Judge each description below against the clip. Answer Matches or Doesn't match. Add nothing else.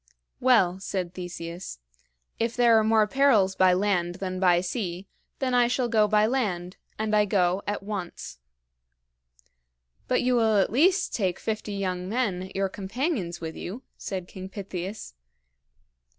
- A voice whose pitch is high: Matches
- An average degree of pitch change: Matches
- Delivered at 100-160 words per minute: Matches